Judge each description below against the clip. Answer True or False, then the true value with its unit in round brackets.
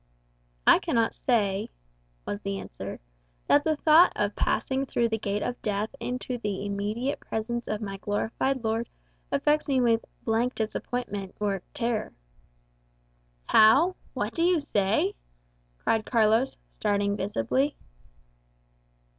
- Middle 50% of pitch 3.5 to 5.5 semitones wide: True (4.0 semitones)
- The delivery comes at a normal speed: False (125 wpm)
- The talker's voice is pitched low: False (225 Hz)